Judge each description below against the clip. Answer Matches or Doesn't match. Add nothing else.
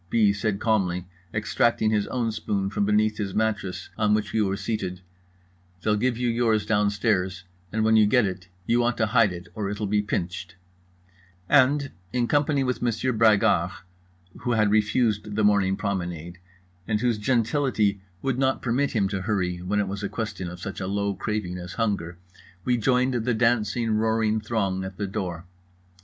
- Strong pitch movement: Doesn't match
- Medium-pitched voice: Doesn't match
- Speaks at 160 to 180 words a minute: Matches